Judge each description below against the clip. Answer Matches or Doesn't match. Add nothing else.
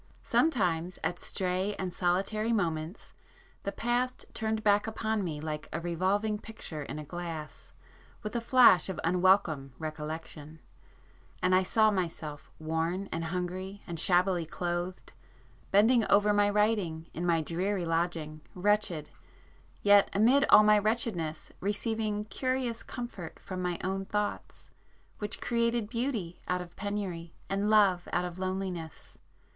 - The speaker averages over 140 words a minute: Doesn't match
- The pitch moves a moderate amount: Matches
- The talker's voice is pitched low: Doesn't match